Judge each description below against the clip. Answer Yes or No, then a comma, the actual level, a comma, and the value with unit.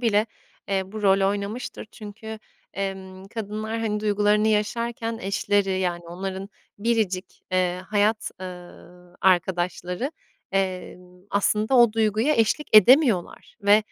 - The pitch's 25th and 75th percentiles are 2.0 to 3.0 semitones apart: Yes, average, 2.7 semitones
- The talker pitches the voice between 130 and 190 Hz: No, high, 205 Hz